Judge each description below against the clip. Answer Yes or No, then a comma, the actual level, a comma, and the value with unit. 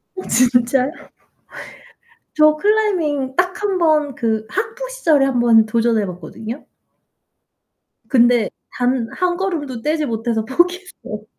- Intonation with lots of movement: Yes, wide, 7.2 semitones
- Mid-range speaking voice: No, very high, 270 Hz